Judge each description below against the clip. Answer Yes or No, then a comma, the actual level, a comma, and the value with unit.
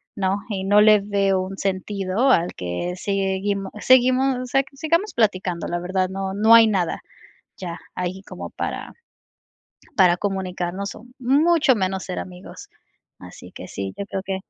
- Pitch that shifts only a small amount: No, average, 3.0 semitones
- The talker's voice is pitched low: No, high, 195 Hz